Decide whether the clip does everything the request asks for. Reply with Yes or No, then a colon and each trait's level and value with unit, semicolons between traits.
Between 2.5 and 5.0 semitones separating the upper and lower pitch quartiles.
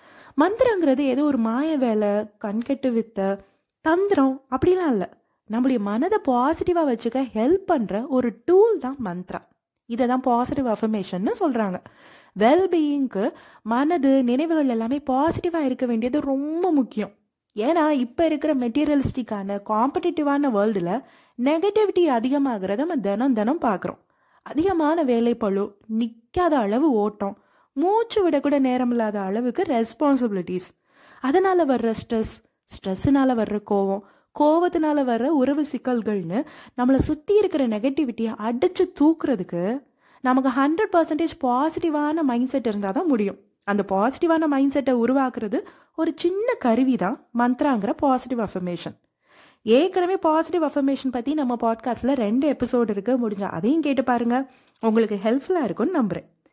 No: wide, 5.5 semitones